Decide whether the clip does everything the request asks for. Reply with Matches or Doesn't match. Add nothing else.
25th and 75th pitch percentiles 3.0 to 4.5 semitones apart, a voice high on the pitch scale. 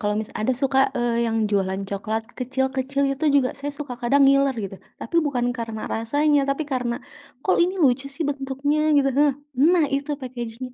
Matches